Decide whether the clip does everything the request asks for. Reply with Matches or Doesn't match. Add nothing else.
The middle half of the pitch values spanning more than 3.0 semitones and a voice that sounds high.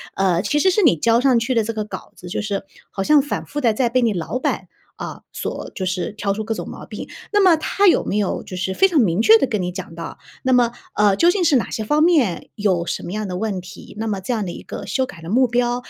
Matches